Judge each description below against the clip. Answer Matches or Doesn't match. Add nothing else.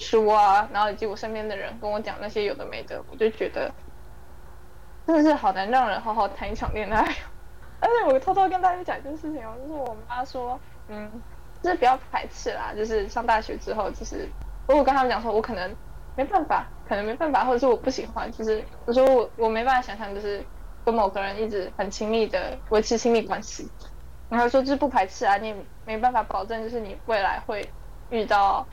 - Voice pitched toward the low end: Doesn't match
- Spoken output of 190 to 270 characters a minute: Doesn't match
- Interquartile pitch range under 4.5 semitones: Matches